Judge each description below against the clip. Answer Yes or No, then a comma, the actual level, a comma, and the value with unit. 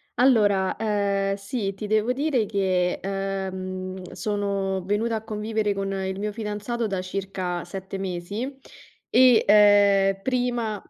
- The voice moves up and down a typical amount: No, narrow, 2.2 semitones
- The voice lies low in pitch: No, high, 200 Hz